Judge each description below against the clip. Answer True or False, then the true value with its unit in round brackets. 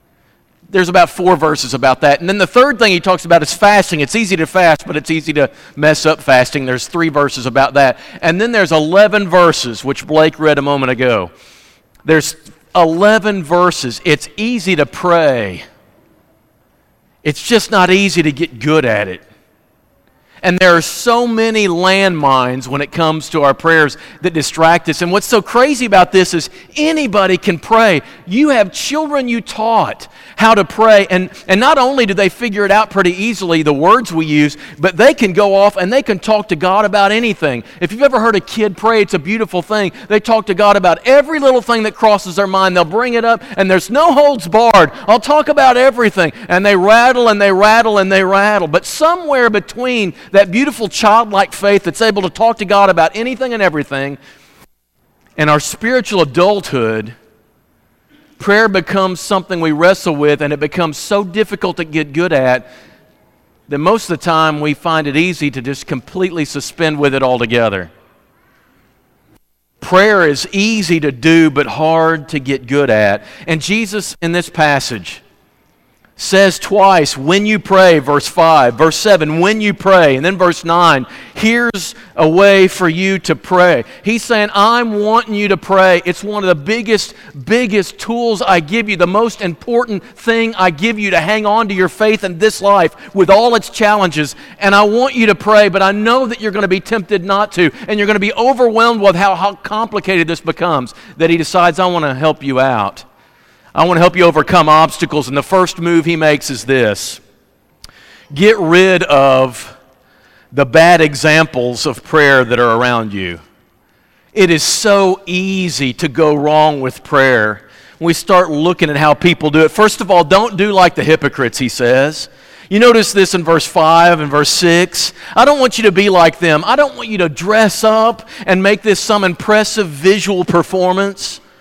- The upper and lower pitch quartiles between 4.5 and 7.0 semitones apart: True (5.2 semitones)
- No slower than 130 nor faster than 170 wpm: False (190 wpm)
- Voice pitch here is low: False (185 Hz)